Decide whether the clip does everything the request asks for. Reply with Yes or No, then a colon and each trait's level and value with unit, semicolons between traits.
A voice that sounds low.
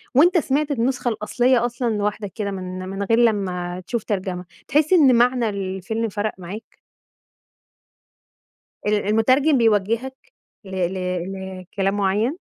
No: high, 215 Hz